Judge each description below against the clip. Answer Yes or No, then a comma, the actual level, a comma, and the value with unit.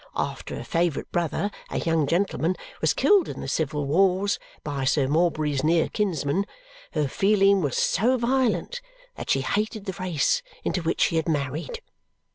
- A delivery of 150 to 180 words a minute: Yes, average, 160 wpm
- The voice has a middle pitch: Yes, medium, 170 Hz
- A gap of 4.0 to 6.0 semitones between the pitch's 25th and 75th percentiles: Yes, average, 5.1 semitones